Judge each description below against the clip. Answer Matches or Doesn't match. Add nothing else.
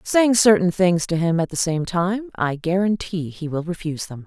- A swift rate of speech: Matches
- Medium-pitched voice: Matches